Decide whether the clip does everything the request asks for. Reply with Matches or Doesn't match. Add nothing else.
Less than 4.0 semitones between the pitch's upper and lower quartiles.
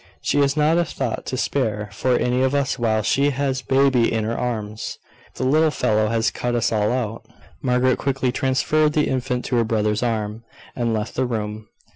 Matches